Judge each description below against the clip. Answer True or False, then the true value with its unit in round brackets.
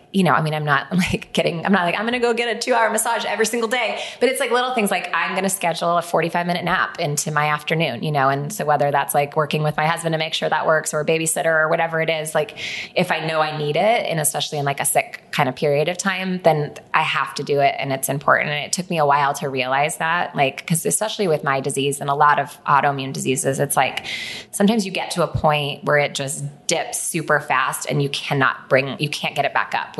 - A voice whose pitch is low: False (155 Hz)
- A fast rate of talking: True (270 wpm)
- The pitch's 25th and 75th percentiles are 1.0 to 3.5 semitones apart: False (4.3 semitones)